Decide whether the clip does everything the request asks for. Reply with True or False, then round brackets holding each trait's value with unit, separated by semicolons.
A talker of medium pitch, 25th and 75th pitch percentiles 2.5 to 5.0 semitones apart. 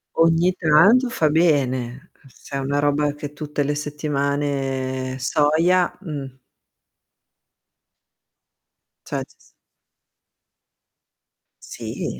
True (145 Hz; 2.8 semitones)